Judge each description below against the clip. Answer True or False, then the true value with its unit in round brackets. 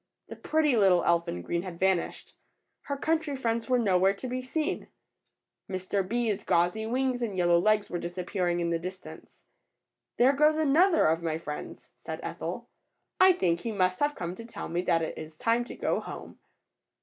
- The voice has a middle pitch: False (195 Hz)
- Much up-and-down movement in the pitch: True (6.5 semitones)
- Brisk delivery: False (185 wpm)